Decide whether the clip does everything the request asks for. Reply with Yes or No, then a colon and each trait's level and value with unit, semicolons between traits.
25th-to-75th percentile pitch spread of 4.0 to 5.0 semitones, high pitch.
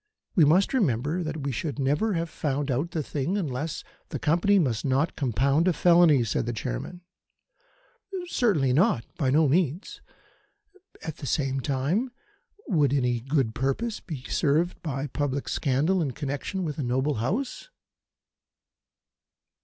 No: average, 4.3 semitones; medium, 145 Hz